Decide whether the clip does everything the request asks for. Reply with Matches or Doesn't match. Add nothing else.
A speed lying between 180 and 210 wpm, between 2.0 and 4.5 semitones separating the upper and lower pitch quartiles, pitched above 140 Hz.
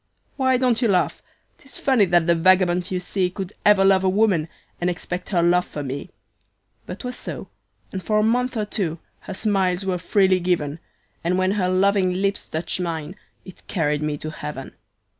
Matches